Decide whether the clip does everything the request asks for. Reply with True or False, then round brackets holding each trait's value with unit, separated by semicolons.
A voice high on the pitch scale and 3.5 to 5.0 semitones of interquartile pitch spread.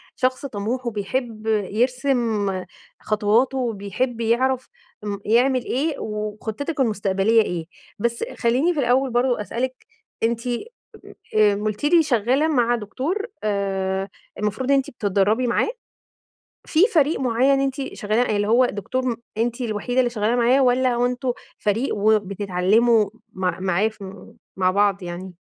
True (230 Hz; 3.9 semitones)